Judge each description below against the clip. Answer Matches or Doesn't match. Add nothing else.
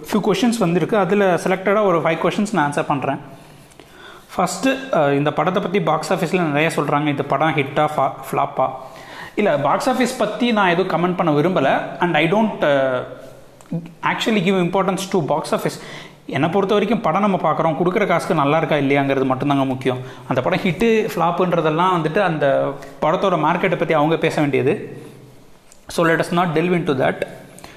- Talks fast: Matches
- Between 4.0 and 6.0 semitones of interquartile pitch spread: Matches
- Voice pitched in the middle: Matches